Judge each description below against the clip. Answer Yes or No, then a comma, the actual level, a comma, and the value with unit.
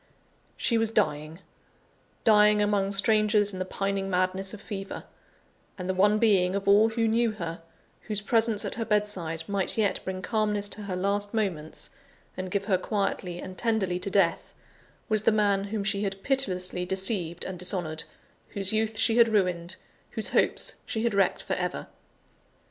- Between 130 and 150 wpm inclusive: No, average, 170 wpm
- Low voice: No, high, 200 Hz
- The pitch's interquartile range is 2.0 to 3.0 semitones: Yes, narrow, 2.5 semitones